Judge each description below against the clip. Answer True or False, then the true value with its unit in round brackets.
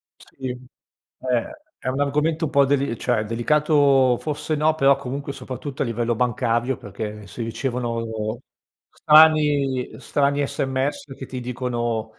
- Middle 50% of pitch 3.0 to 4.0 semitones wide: True (3.3 semitones)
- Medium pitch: False (130 Hz)